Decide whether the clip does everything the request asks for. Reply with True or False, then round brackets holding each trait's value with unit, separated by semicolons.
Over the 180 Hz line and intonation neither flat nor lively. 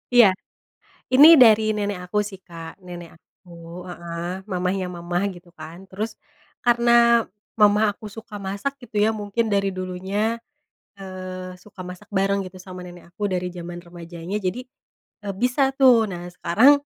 True (190 Hz; 3.3 semitones)